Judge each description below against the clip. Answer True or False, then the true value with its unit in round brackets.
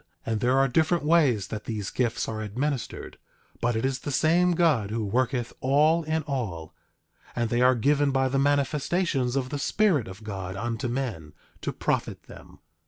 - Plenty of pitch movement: False (4.5 semitones)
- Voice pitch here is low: True (130 Hz)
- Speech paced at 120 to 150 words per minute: False (175 wpm)